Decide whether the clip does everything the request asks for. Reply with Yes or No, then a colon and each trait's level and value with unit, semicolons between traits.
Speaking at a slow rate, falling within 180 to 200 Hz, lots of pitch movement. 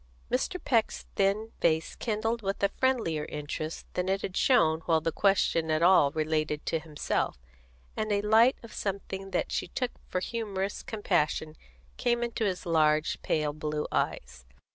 No: average, 160 wpm; high, 190 Hz; wide, 5.7 semitones